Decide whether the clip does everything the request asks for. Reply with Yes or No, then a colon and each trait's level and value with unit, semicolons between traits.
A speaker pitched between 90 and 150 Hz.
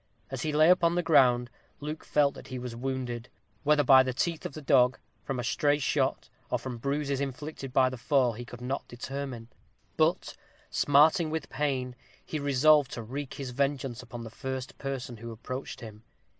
Yes: low, 135 Hz